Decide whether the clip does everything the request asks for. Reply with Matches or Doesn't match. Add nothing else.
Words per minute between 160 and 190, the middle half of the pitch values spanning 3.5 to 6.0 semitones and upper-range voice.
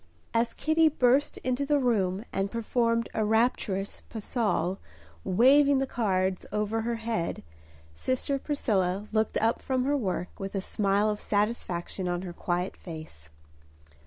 Doesn't match